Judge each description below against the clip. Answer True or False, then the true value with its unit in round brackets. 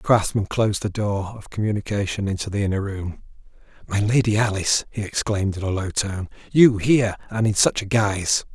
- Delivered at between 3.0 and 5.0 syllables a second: False (5.7 syllables/s)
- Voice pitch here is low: True (105 Hz)